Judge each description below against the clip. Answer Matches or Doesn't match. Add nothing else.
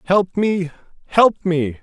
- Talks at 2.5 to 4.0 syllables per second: Matches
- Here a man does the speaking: Matches